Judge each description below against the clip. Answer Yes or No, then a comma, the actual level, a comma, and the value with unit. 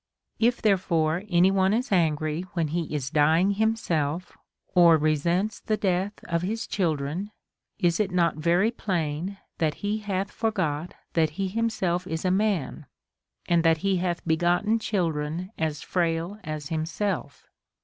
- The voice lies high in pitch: No, medium, 175 Hz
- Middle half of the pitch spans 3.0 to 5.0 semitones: Yes, average, 3.7 semitones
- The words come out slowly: No, average, 145 wpm